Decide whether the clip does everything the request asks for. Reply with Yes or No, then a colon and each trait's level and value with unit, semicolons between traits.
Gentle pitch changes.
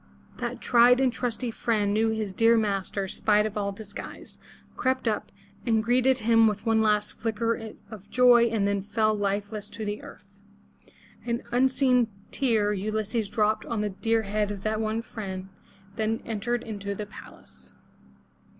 Yes: narrow, 2.0 semitones